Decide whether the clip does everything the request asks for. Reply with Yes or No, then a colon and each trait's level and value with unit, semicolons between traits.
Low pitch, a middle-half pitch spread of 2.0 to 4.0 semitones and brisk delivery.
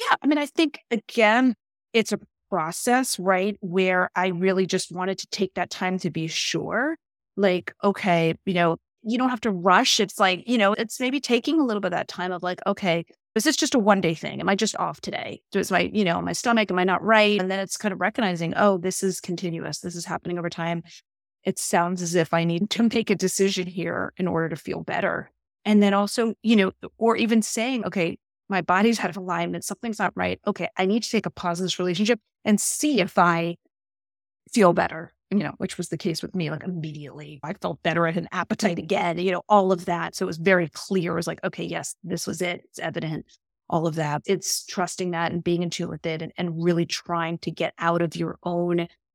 No: medium, 185 Hz; average, 3.4 semitones; fast, 235 wpm